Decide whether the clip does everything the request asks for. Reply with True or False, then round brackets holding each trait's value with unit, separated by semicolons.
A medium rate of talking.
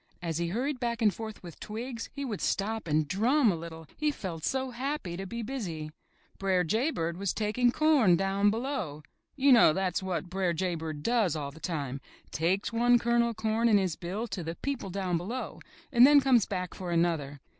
False (210 wpm)